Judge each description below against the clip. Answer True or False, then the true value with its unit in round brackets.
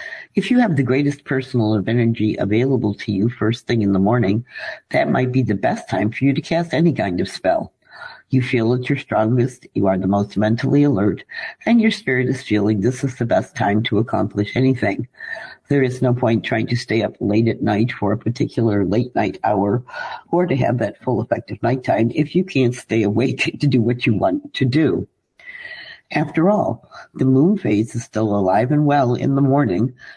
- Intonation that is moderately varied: True (4.3 semitones)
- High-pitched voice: False (120 Hz)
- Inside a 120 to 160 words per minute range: False (205 wpm)